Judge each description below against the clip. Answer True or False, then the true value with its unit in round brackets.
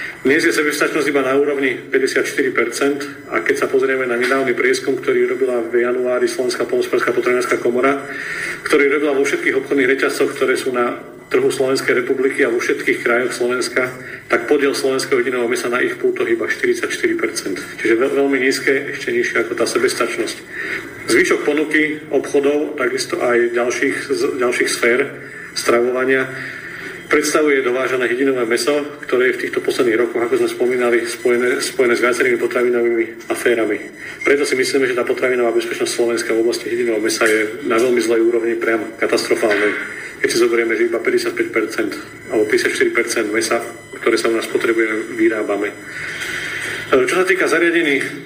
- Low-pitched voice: False (365 Hz)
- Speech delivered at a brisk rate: False (155 wpm)